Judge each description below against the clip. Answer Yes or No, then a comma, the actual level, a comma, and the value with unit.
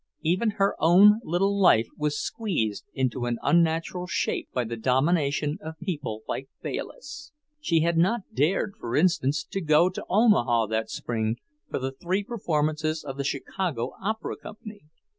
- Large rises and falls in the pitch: Yes, wide, 6.4 semitones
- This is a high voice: No, medium, 160 Hz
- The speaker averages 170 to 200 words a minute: No, average, 155 wpm